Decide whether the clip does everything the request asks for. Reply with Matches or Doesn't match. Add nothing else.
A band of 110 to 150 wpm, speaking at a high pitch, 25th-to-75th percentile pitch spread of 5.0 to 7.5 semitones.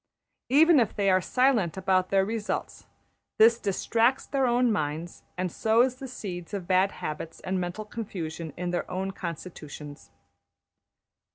Doesn't match